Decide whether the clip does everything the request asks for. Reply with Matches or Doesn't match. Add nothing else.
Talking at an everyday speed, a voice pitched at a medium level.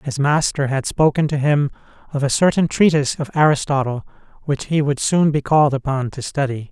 Matches